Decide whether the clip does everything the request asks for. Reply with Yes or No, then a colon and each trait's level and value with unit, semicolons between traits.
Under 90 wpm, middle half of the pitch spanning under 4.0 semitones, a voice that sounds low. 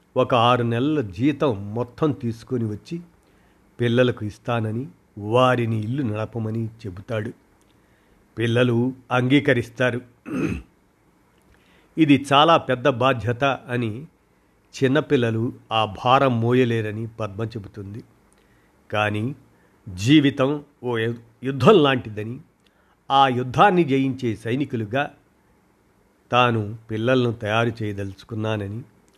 Yes: average, 80 wpm; average, 3.2 semitones; low, 120 Hz